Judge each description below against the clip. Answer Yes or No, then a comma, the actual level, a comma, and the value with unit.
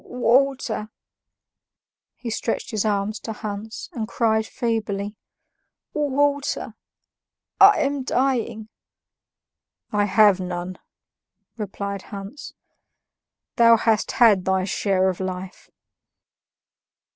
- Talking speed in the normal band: No, slow, 90 wpm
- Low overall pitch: No, high, 220 Hz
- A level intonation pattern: No, average, 3.4 semitones